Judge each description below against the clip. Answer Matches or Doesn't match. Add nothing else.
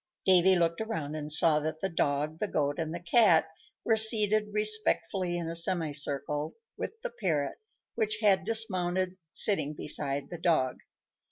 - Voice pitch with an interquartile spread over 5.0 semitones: Matches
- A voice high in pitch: Doesn't match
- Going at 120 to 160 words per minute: Matches